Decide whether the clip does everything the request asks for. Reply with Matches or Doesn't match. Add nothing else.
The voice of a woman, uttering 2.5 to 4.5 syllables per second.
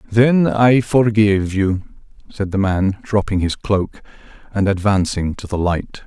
Doesn't match